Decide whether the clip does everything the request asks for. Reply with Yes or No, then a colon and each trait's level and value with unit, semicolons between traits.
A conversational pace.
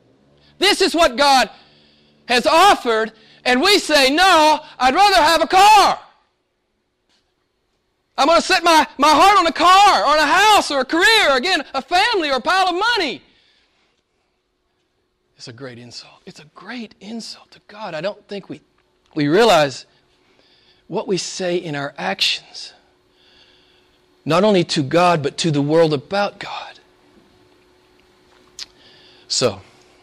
Yes: average, 145 wpm